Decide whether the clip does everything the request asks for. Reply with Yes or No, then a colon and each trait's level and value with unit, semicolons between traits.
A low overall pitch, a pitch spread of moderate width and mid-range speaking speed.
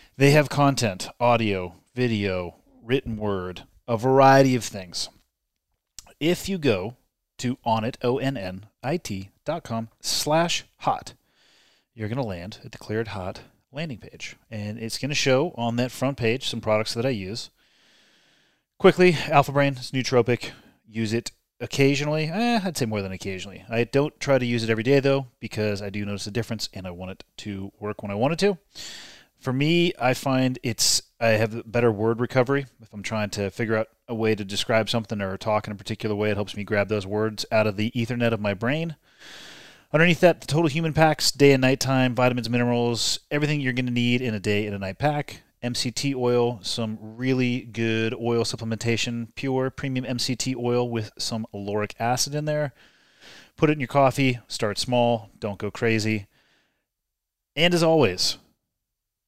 Yes: low, 115 Hz; average, 3.9 semitones; average, 180 wpm